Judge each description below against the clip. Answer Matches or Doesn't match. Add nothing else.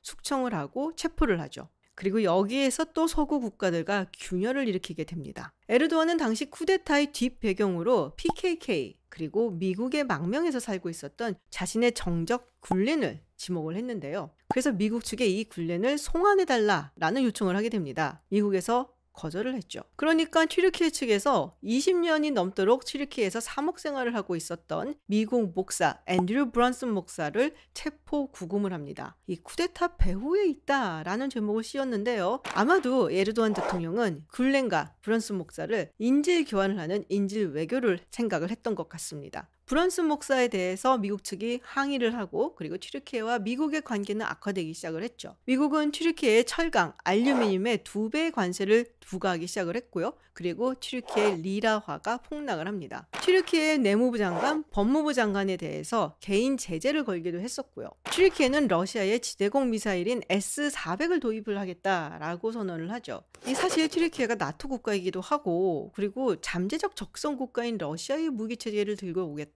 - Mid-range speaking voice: Doesn't match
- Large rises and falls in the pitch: Matches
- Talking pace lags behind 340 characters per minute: Doesn't match